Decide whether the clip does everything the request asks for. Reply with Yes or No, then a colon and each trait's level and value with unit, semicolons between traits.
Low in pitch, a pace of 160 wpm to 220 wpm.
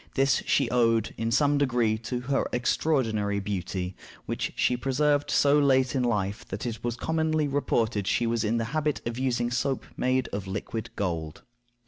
Yes: low, 120 Hz; average, 170 wpm